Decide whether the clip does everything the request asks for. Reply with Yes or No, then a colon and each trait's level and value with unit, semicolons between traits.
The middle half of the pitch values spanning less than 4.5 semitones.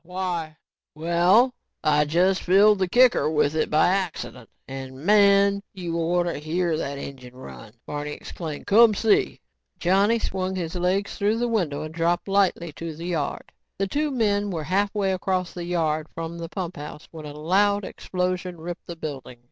Yes: average, 3.9 semitones